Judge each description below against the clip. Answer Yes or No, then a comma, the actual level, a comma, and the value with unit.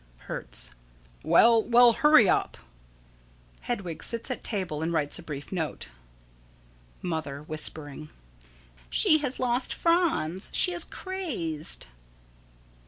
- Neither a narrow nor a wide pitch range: No, wide, 8.5 semitones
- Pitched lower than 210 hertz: Yes, medium, 185 Hz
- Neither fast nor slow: No, slow, 105 wpm